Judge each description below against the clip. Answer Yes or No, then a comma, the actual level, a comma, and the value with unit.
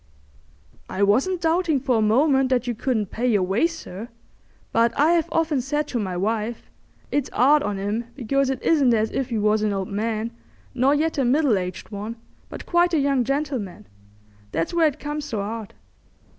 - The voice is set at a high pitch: Yes, high, 245 Hz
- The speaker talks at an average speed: Yes, average, 190 wpm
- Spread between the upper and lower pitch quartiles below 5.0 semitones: No, wide, 5.4 semitones